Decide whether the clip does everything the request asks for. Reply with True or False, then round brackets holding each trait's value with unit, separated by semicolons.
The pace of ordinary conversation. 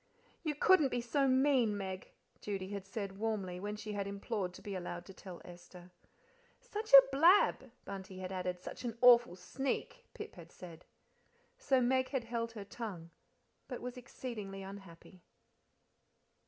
True (155 wpm)